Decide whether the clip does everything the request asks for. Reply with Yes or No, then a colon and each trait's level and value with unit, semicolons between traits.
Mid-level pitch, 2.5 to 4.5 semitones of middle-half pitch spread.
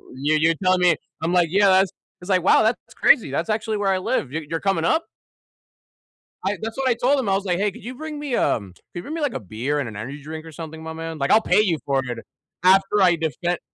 No: medium, 180 Hz; average, 5.0 semitones